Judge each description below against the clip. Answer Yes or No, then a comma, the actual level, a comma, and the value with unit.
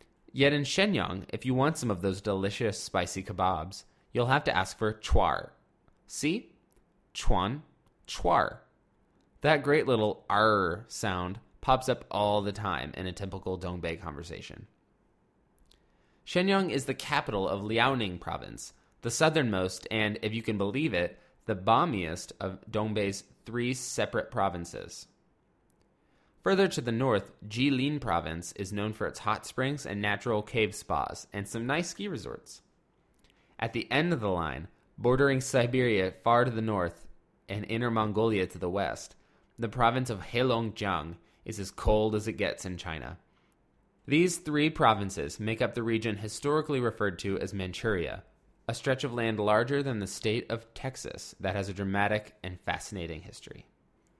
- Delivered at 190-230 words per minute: No, average, 155 wpm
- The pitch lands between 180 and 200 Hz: No, low, 110 Hz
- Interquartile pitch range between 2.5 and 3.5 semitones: No, average, 4.6 semitones